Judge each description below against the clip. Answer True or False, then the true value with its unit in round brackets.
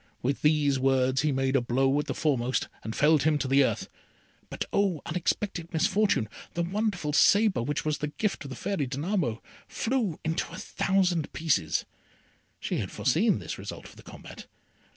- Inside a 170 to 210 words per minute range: True (175 wpm)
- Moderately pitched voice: True (150 Hz)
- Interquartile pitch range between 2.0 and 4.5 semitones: False (5.2 semitones)